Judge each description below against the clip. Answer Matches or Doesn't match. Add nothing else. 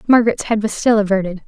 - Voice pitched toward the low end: Doesn't match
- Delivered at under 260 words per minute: Matches